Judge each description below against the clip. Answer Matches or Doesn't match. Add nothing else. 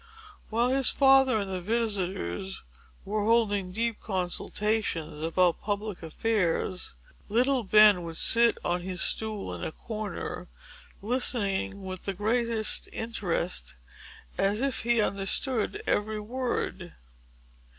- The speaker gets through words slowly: Matches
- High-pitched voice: Matches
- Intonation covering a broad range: Doesn't match